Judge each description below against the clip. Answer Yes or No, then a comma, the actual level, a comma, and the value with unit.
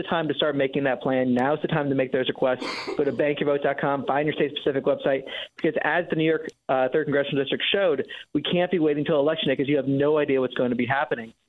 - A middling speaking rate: No, fast, 255 wpm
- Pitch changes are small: Yes, narrow, 2.1 semitones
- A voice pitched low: No, medium, 145 Hz